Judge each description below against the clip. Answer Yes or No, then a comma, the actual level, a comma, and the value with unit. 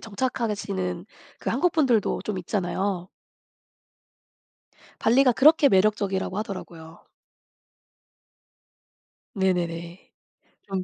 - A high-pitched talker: Yes, high, 195 Hz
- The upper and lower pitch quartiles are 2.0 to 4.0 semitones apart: Yes, average, 3.7 semitones